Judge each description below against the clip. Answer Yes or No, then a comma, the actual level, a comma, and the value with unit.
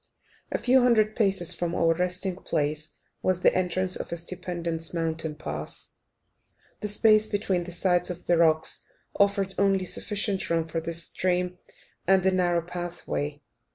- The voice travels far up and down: No, narrow, 2.5 semitones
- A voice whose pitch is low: No, medium, 180 Hz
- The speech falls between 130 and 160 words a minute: Yes, average, 155 wpm